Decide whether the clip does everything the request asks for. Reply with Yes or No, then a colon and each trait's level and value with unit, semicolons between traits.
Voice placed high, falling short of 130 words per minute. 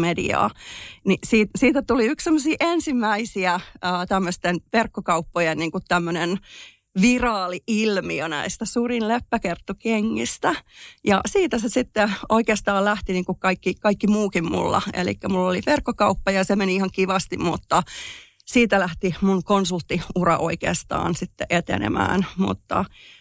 Yes: high, 195 Hz; average, 115 wpm